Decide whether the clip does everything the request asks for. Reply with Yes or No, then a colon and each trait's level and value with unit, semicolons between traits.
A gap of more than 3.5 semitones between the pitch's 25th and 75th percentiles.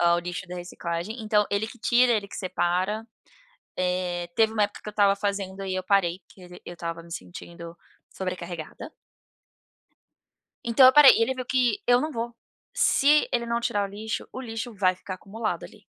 Yes: average, 4.4 semitones